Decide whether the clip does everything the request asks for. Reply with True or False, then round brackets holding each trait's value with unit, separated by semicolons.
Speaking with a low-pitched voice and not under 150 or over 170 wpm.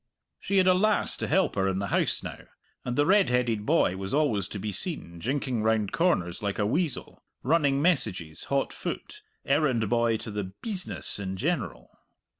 False (120 Hz; 185 wpm)